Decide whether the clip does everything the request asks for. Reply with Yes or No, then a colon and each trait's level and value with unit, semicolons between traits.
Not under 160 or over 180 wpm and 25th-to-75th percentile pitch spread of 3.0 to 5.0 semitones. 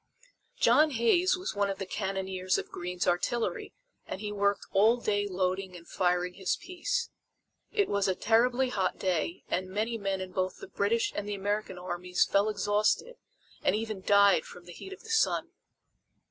Yes: average, 175 wpm; average, 3.4 semitones